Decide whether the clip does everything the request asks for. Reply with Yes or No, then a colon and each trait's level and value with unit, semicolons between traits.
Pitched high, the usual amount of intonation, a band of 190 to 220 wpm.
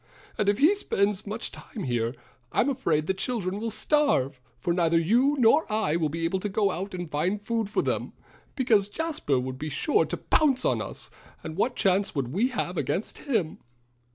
No: high, 200 Hz; wide, 6.2 semitones; average, 195 wpm